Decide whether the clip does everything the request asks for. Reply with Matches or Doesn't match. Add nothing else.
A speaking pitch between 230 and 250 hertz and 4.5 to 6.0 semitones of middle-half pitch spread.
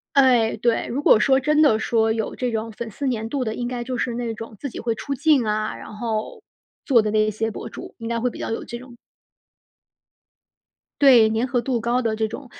Doesn't match